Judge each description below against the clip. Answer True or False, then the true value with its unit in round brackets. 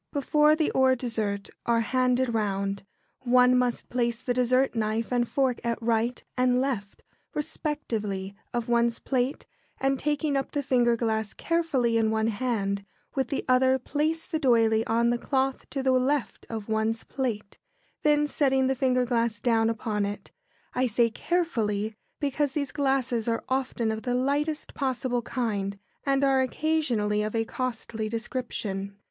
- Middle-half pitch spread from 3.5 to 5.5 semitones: False (3.1 semitones)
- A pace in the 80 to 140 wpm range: False (160 wpm)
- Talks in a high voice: True (245 Hz)